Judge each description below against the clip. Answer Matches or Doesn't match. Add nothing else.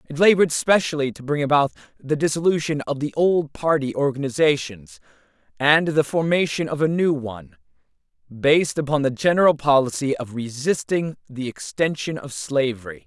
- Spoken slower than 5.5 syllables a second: Matches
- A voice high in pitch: Doesn't match